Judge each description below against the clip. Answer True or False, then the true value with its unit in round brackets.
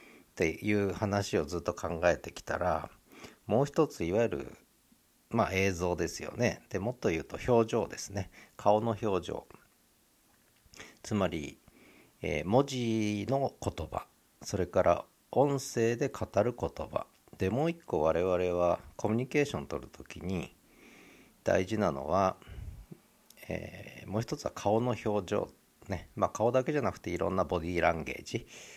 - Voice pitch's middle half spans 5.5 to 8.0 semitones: False (5.1 semitones)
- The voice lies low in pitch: True (105 Hz)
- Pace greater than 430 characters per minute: False (270 characters per minute)